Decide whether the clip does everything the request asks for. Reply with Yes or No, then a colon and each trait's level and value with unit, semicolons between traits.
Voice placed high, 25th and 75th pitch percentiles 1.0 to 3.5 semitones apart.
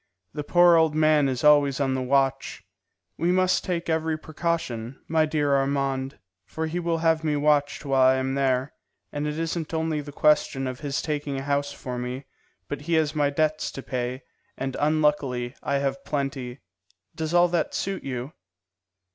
No: medium, 145 Hz; average, 2.8 semitones